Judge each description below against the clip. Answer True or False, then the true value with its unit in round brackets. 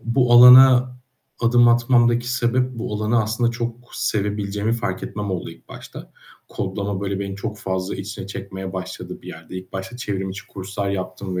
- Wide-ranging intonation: False (3.7 semitones)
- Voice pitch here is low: True (105 Hz)